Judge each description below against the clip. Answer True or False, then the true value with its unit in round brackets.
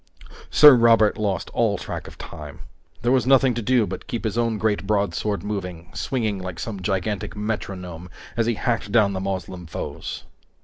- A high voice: False (105 Hz)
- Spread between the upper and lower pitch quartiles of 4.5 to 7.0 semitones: False (3.8 semitones)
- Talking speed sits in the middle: True (175 wpm)